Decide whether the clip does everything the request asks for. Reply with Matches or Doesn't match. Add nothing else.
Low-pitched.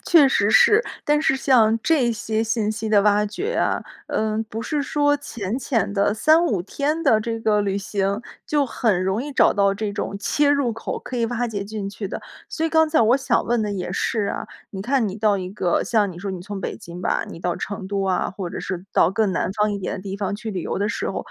Doesn't match